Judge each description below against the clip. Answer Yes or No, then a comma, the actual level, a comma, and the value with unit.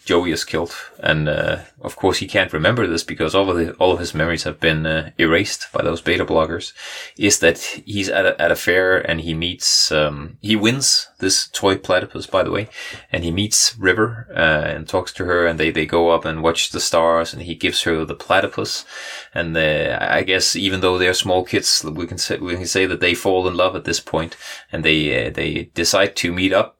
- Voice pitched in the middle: No, very low, 85 Hz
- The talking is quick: Yes, fast, 230 wpm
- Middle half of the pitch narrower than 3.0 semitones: Yes, narrow, 2.4 semitones